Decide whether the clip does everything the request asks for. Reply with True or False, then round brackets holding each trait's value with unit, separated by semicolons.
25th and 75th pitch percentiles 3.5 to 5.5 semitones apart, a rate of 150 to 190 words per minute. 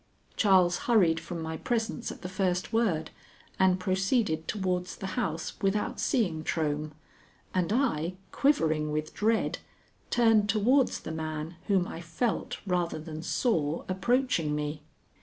False (5.1 semitones; 135 wpm)